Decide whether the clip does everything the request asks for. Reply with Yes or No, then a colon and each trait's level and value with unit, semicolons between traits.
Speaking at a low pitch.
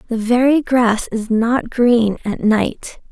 No: high, 235 Hz